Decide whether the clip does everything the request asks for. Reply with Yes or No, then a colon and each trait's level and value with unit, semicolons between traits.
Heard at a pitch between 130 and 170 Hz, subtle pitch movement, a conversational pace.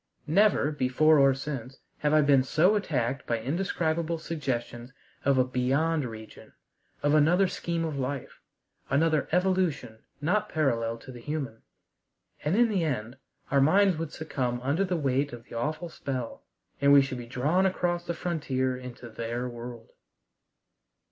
No: medium, 140 Hz; average, 4.5 semitones; average, 155 wpm